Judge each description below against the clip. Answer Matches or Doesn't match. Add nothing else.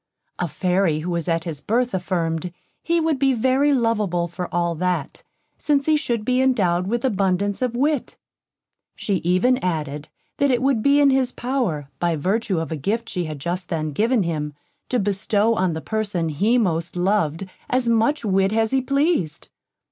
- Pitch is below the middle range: Doesn't match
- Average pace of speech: Matches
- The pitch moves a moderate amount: Doesn't match